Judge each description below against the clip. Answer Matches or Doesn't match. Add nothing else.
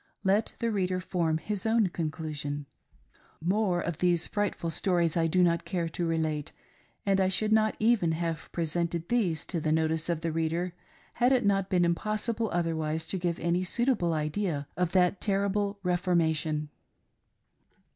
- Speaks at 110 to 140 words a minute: Doesn't match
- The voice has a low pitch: Doesn't match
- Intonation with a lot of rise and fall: Doesn't match